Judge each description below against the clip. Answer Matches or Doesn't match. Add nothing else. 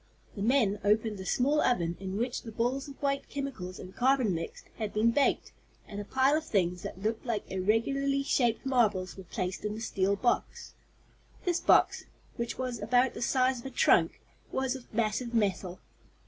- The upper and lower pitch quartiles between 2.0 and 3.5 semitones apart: Doesn't match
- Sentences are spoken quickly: Doesn't match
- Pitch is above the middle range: Matches